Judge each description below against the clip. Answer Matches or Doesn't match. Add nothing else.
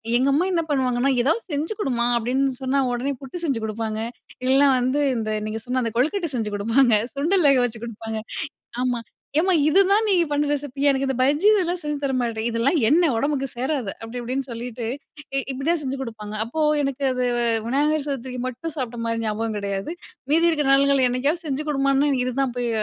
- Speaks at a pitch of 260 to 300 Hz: Matches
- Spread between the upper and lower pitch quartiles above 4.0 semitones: Doesn't match